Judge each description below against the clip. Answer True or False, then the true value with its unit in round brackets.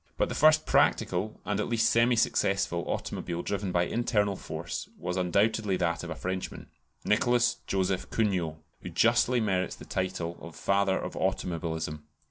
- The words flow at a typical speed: True (155 wpm)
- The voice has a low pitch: True (95 Hz)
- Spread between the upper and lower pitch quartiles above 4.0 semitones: False (3.7 semitones)